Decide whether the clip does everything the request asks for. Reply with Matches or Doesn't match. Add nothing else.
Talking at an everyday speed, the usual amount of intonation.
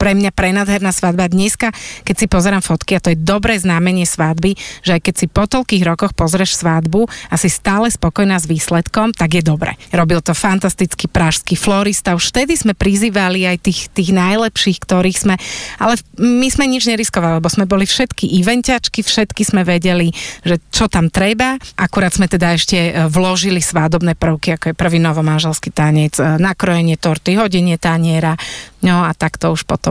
Doesn't match